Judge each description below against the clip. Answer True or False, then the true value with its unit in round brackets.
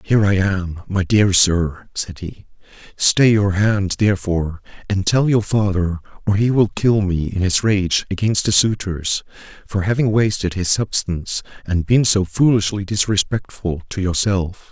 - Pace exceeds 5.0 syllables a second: False (4.4 syllables/s)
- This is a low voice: True (100 Hz)